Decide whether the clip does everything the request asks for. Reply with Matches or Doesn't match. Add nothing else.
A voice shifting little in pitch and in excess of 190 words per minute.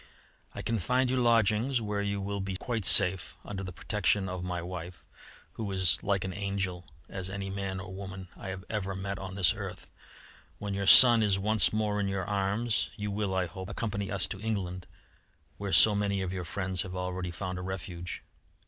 Matches